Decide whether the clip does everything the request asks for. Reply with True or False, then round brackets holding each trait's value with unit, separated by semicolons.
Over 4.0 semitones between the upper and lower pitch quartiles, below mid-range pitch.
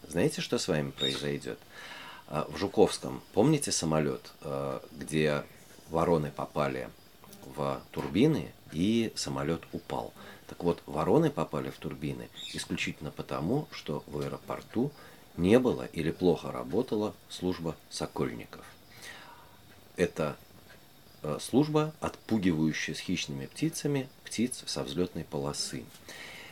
True (5.4 semitones; 80 Hz)